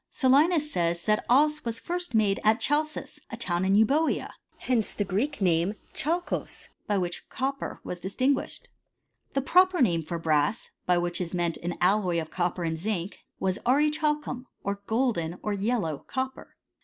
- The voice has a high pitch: Yes, high, 215 Hz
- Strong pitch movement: Yes, wide, 7.6 semitones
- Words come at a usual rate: Yes, average, 165 wpm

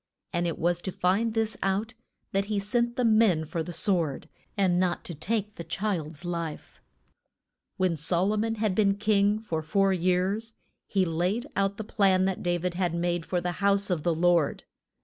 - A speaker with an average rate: No, fast, 215 wpm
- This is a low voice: No, medium, 185 Hz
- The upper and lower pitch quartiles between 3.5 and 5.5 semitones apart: No, average, 3.1 semitones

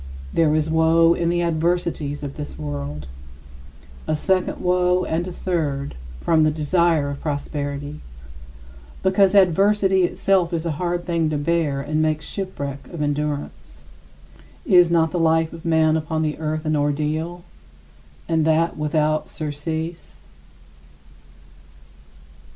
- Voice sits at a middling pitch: Yes, medium, 160 Hz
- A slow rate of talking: Yes, slow, 130 wpm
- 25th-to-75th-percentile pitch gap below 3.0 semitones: Yes, narrow, 2.4 semitones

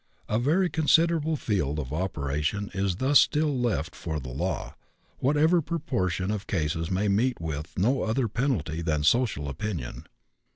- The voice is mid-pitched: No, low, 100 Hz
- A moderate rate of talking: Yes, average, 150 wpm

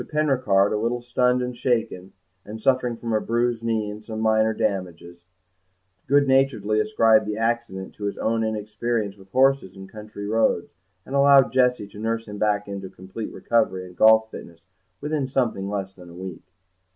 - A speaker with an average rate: Yes, average, 175 wpm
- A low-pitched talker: Yes, low, 110 Hz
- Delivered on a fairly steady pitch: No, average, 3.2 semitones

